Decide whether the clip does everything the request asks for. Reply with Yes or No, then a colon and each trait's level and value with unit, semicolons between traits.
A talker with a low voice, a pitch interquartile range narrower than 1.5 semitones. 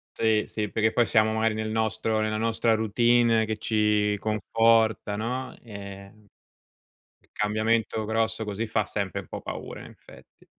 Yes: low, 110 Hz; narrow, 1.0 semitones